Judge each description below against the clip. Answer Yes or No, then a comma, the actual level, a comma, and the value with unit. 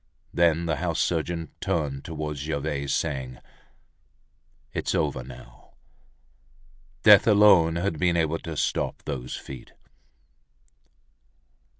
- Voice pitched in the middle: No, very low, 80 Hz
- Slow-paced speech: Yes, slow, 100 wpm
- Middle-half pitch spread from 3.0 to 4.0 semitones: Yes, average, 3.3 semitones